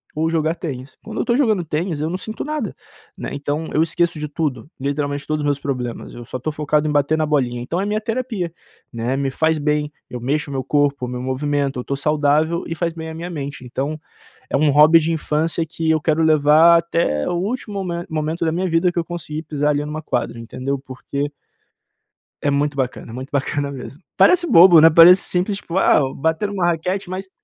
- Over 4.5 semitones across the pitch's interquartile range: No, average, 3.2 semitones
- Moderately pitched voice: Yes, medium, 155 Hz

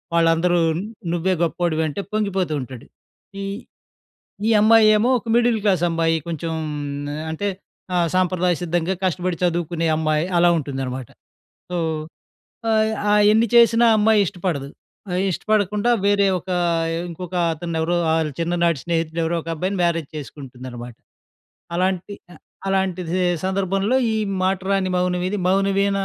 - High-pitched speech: No, medium, 180 Hz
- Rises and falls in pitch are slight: No, average, 3.2 semitones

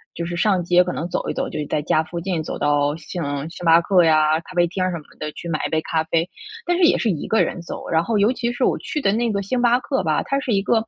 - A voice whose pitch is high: No, medium, 175 Hz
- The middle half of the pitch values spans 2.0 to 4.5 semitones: No, wide, 5.4 semitones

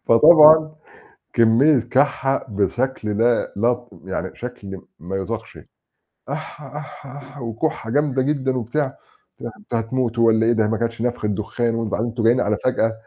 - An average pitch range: Yes, average, 3.2 semitones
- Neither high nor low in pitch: No, low, 120 Hz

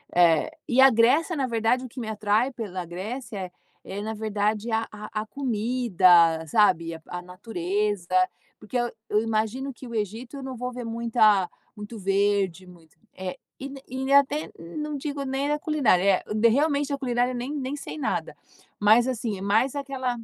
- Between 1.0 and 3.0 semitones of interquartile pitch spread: No, average, 4.4 semitones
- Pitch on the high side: Yes, high, 225 Hz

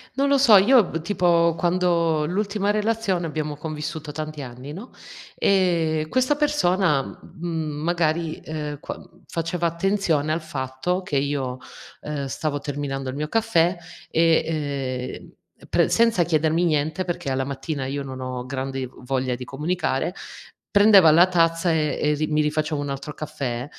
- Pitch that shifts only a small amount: No, average, 3.7 semitones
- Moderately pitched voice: Yes, medium, 155 Hz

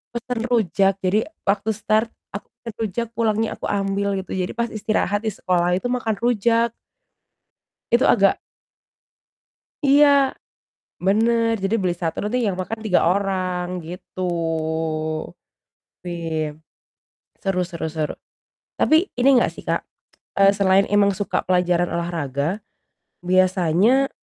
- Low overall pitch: No, high, 195 Hz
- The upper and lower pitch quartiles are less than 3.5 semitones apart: No, average, 3.8 semitones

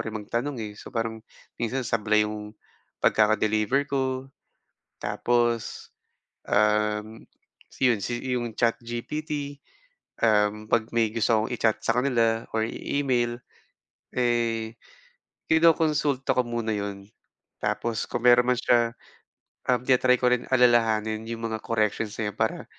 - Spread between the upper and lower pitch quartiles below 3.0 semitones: Yes, narrow, 2.5 semitones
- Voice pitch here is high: No, low, 115 Hz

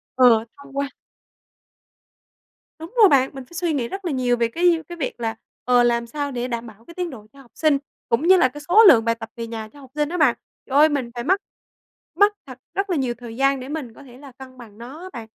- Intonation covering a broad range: No, average, 4.8 semitones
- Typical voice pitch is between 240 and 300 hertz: Yes, very high, 265 Hz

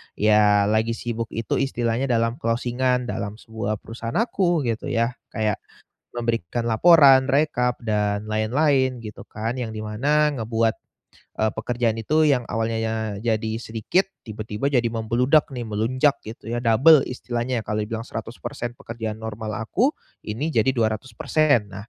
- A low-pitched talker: Yes, low, 115 Hz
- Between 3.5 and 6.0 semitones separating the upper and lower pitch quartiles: No, narrow, 2.6 semitones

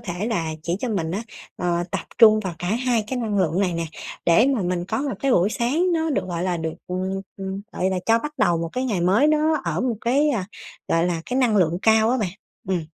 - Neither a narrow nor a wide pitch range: No, wide, 5.9 semitones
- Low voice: No, high, 200 Hz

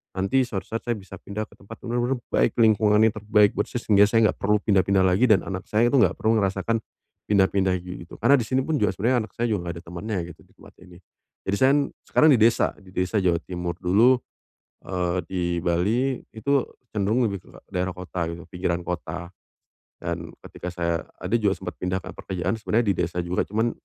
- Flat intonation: No, average, 3.7 semitones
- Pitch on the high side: No, low, 100 Hz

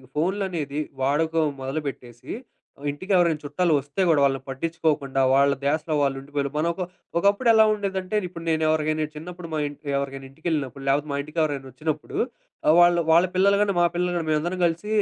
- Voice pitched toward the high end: No, medium, 155 Hz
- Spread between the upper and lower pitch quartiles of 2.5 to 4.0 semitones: Yes, average, 3.7 semitones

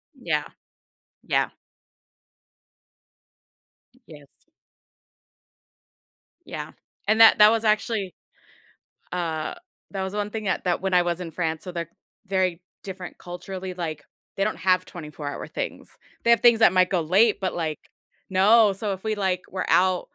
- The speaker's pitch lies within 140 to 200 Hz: Yes, medium, 185 Hz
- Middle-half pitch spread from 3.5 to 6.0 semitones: No, average, 2.9 semitones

